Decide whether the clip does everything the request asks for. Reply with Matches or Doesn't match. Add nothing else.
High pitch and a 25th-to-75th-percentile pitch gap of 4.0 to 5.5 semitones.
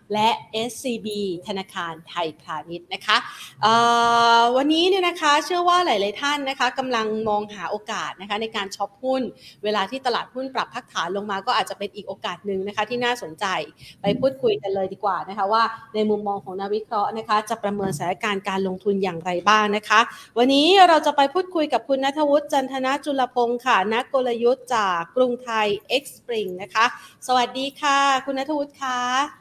Matches